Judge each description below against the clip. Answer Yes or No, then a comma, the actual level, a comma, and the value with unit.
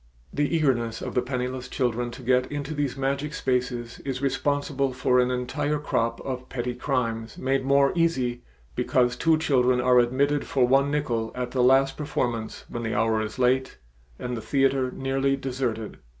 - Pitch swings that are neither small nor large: No, narrow, 2.0 semitones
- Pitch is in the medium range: No, low, 130 Hz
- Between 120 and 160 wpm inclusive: No, average, 170 wpm